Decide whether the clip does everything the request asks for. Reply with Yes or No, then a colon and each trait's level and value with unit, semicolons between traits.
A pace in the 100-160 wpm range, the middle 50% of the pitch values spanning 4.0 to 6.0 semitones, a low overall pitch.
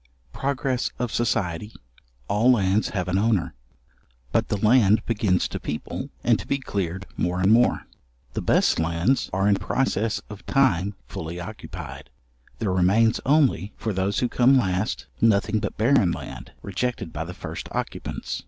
Yes: average, 155 wpm; average, 4.5 semitones; low, 105 Hz